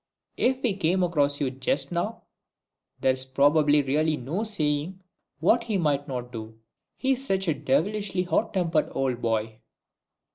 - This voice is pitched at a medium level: Yes, medium, 155 Hz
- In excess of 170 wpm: No, slow, 135 wpm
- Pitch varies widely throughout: Yes, wide, 6.0 semitones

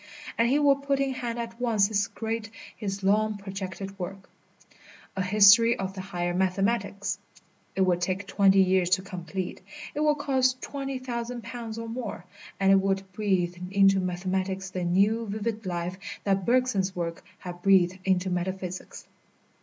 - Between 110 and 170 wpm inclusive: Yes, average, 160 wpm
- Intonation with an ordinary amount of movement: Yes, average, 3.5 semitones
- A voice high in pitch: Yes, high, 195 Hz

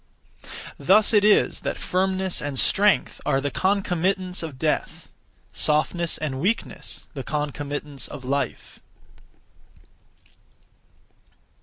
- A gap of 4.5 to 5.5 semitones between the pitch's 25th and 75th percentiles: Yes, average, 4.8 semitones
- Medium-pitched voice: Yes, medium, 165 Hz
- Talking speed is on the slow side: Yes, slow, 100 wpm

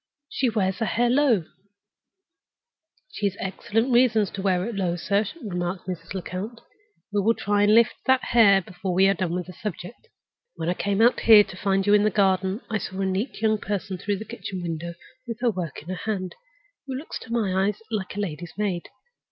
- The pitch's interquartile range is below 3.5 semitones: Yes, average, 2.9 semitones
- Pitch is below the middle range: No, high, 200 Hz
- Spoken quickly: Yes, fast, 210 wpm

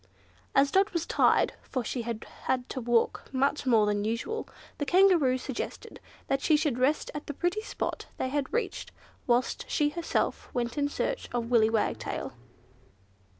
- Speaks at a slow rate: No, average, 165 wpm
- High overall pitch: Yes, very high, 265 Hz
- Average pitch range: Yes, average, 4.5 semitones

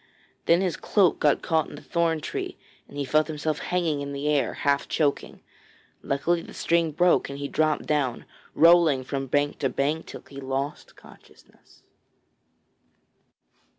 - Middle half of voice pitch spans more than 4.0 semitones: No, average, 2.8 semitones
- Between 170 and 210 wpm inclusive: No, average, 155 wpm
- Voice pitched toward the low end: No, medium, 150 Hz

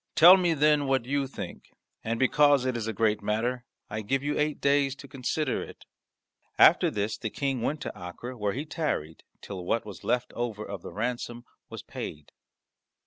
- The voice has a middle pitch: No, low, 125 Hz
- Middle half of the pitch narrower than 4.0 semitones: No, average, 4.7 semitones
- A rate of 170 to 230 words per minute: Yes, average, 190 wpm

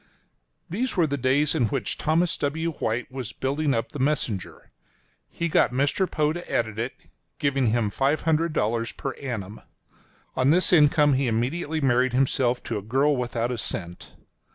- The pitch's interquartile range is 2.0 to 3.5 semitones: No, average, 4.2 semitones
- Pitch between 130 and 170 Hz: Yes, low, 135 Hz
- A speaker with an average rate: Yes, average, 160 wpm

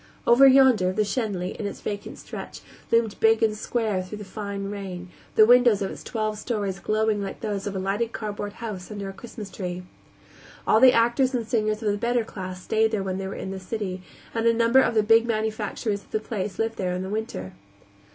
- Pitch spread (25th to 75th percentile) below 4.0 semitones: Yes, narrow, 2.6 semitones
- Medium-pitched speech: No, high, 215 Hz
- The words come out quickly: Yes, fast, 220 wpm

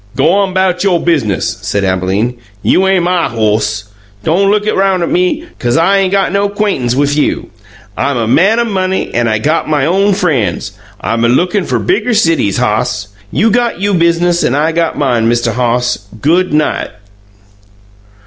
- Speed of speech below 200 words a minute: Yes, average, 170 wpm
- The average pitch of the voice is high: No, medium, 165 Hz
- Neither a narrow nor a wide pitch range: No, wide, 8.0 semitones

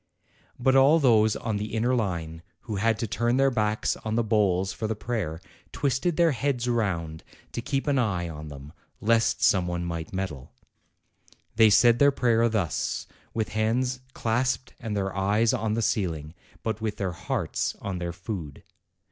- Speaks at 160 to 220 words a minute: Yes, average, 175 wpm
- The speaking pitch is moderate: No, low, 110 Hz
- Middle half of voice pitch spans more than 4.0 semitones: Yes, average, 4.5 semitones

